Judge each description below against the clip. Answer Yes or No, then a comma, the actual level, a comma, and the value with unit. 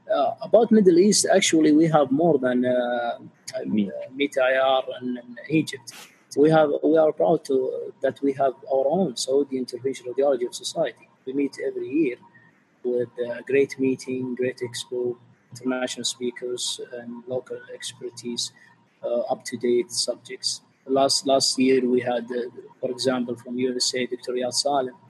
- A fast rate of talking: No, average, 155 wpm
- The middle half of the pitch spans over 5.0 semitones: No, average, 3.7 semitones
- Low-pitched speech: Yes, low, 130 Hz